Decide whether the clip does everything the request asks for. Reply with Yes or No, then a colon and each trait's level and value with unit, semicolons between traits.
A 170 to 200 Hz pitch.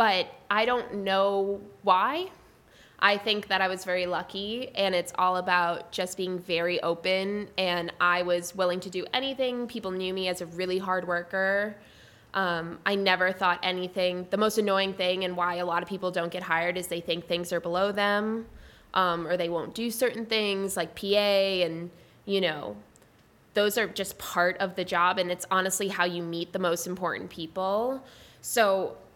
Yes: medium, 185 Hz